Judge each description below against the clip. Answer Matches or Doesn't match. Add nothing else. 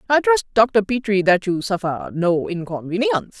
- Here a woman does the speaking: Matches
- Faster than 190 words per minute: Doesn't match